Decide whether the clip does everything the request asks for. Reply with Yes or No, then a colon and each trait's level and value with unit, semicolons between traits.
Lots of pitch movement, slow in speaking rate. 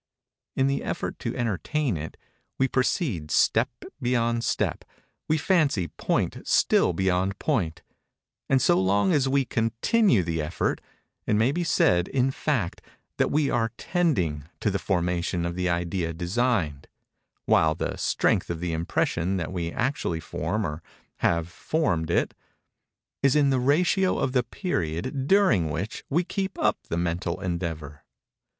No: wide, 7.9 semitones; average, 145 wpm